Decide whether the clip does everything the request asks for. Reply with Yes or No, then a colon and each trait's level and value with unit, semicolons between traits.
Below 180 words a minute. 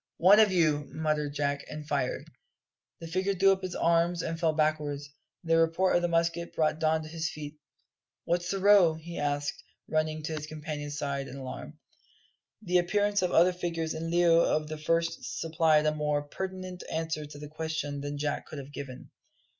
No: average, 185 wpm